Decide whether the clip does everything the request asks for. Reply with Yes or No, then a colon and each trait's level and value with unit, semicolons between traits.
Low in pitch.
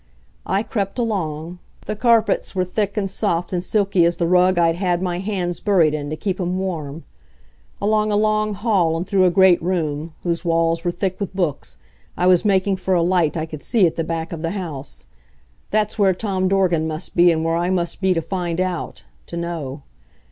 No: medium, 180 Hz